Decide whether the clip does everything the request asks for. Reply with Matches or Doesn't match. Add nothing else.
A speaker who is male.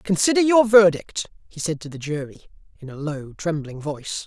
Matches